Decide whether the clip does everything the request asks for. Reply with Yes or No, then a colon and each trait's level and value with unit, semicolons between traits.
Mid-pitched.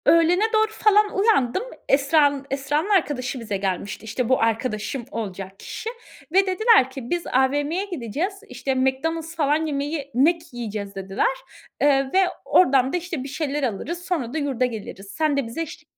No: very high, 280 Hz